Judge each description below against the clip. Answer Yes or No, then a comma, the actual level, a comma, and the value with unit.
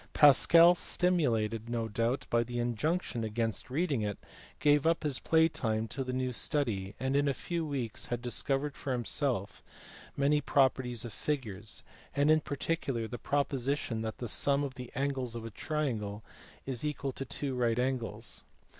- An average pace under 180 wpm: Yes, average, 165 wpm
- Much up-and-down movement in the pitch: No, average, 3.9 semitones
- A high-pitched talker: No, low, 130 Hz